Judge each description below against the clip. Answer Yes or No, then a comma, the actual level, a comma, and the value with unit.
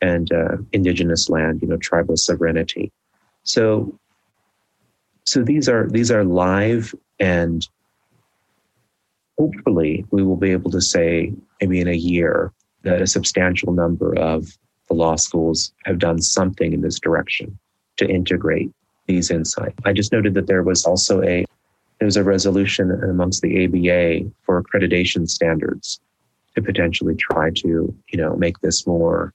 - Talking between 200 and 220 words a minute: No, average, 145 wpm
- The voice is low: Yes, very low, 90 Hz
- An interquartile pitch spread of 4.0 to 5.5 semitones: No, narrow, 2.6 semitones